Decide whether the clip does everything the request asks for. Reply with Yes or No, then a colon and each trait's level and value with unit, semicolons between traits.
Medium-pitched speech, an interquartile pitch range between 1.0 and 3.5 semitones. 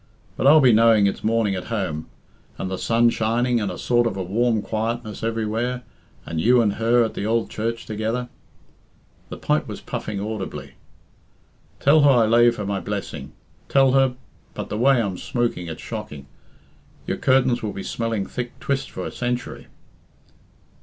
No: low, 115 Hz; average, 2.8 semitones